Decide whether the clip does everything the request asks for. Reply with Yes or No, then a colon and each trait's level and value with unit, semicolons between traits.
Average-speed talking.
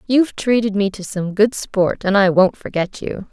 No: fast, 215 wpm